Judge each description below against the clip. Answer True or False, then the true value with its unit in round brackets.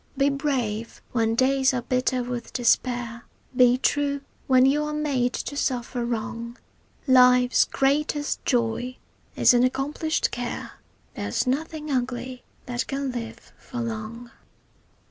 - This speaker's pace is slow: True (125 wpm)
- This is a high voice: True (250 Hz)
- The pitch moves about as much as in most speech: False (2.3 semitones)